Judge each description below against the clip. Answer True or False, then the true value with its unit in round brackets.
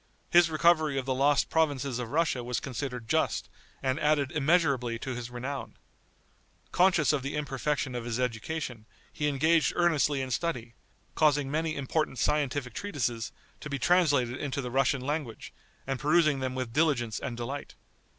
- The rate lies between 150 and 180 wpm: True (160 wpm)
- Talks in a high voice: False (140 Hz)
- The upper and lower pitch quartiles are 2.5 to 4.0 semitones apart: True (3.5 semitones)